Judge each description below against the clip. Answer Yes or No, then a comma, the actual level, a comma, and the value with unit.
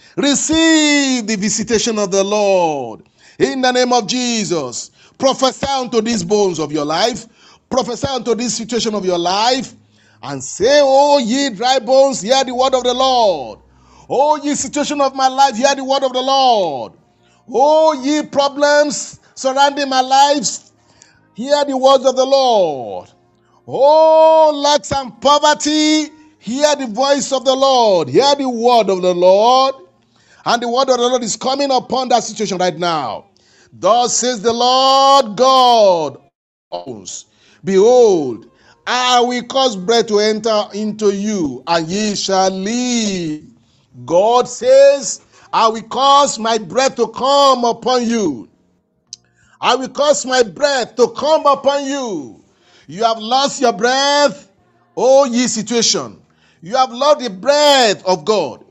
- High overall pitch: Yes, very high, 255 Hz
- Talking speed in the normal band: Yes, average, 145 wpm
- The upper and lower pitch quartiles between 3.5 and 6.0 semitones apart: Yes, average, 3.9 semitones